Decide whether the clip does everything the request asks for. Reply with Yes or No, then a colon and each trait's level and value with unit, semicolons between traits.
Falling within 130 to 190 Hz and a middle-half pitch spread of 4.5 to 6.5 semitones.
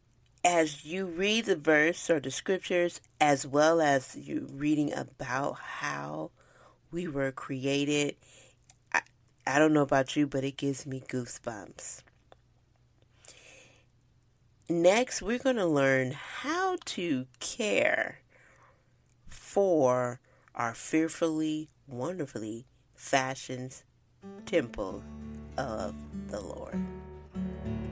Yes: low, 135 Hz; average, 5.2 semitones